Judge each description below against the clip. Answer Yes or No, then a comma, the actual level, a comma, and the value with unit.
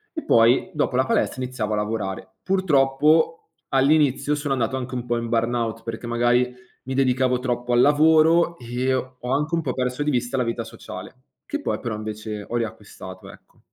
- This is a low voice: Yes, low, 125 Hz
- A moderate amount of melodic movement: Yes, average, 3.7 semitones